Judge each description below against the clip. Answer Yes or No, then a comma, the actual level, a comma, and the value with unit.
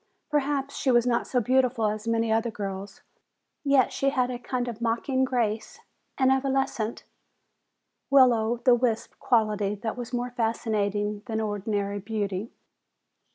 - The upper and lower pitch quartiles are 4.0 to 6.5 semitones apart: No, average, 3.1 semitones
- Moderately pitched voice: No, high, 230 Hz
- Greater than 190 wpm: No, average, 145 wpm